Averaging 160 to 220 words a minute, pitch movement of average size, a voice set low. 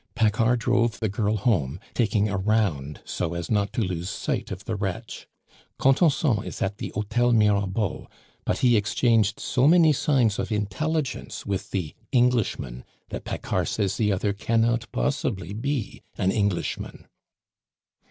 No: average, 145 wpm; average, 3.5 semitones; low, 110 Hz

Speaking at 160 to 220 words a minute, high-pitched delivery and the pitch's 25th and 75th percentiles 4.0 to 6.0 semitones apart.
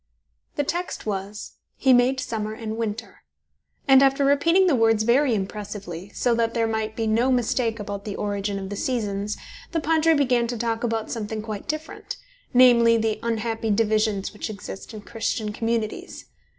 No: average, 165 wpm; high, 225 Hz; average, 2.8 semitones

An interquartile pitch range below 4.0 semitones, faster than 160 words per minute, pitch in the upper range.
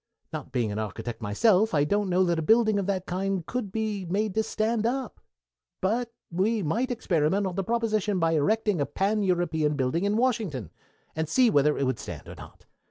No: wide, 5.6 semitones; average, 200 wpm; high, 195 Hz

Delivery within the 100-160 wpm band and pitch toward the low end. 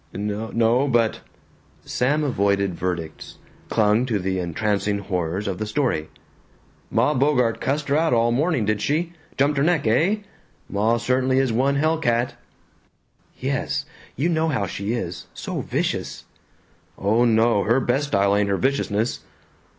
Yes: average, 150 wpm; low, 115 Hz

